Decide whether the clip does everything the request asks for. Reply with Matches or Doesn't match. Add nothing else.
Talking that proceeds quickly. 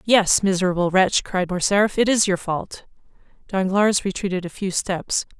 Doesn't match